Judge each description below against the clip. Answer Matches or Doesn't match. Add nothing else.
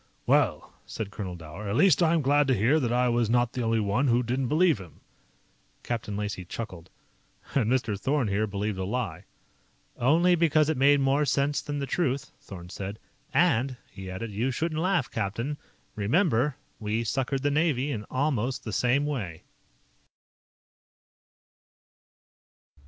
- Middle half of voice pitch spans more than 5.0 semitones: Matches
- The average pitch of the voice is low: Matches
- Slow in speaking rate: Doesn't match